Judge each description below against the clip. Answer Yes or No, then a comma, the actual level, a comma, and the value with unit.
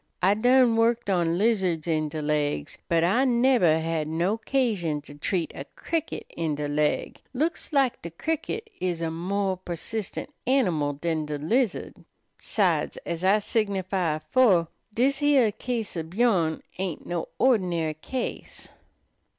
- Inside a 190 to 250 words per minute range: No, average, 145 wpm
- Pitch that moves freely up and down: Yes, wide, 6.7 semitones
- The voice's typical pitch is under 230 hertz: Yes, medium, 185 Hz